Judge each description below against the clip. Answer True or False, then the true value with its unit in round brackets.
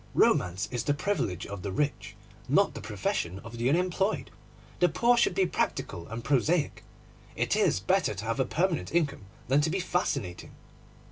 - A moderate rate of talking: True (175 wpm)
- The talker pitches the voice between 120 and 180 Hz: True (140 Hz)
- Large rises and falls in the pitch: True (9.0 semitones)